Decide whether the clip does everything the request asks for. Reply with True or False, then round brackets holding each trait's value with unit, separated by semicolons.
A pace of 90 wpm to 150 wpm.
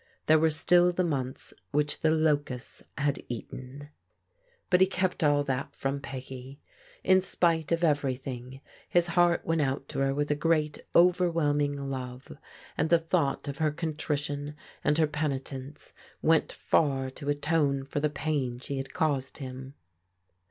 False (160 wpm)